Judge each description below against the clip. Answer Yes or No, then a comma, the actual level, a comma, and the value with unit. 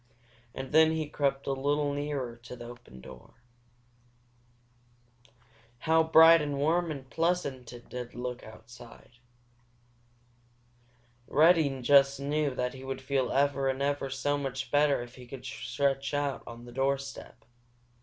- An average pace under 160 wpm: Yes, average, 140 wpm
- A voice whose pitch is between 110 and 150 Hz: Yes, low, 135 Hz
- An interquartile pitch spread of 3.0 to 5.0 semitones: No, narrow, 2.5 semitones